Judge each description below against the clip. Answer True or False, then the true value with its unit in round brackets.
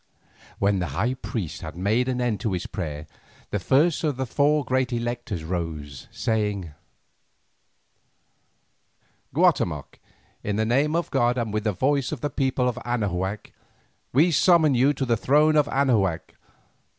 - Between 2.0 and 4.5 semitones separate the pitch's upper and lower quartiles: False (5.5 semitones)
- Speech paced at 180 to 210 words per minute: False (150 wpm)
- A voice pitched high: False (120 Hz)